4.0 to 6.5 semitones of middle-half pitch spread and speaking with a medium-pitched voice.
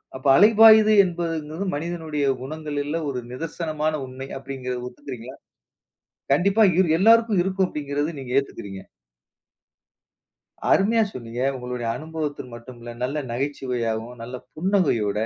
Yes: wide, 5.4 semitones; medium, 145 Hz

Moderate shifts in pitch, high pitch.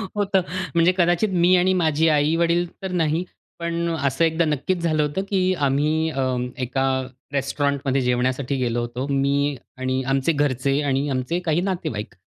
No: average, 3.9 semitones; medium, 150 Hz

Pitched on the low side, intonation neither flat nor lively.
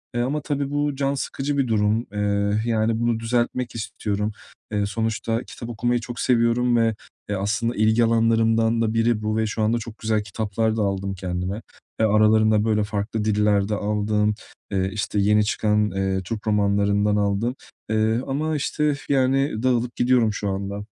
No: low, 110 Hz; narrow, 2.2 semitones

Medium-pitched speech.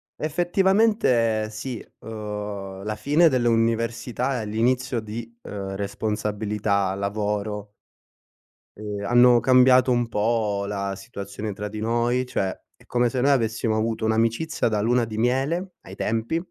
No: low, 115 Hz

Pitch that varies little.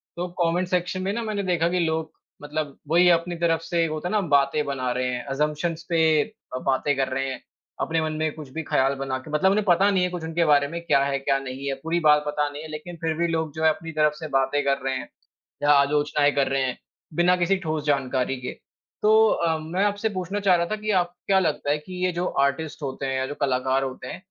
No: average, 3.6 semitones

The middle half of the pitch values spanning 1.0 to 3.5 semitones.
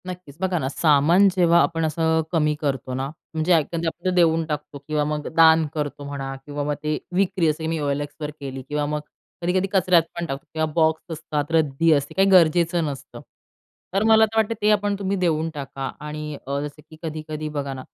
Yes: average, 2.7 semitones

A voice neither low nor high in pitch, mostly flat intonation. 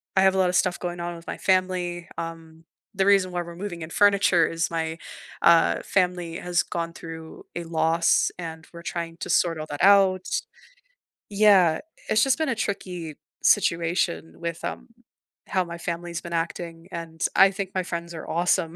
Yes: medium, 170 Hz; narrow, 1.9 semitones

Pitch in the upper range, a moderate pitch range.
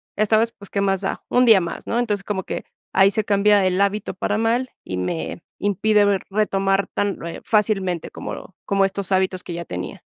No: high, 200 Hz; narrow, 1.9 semitones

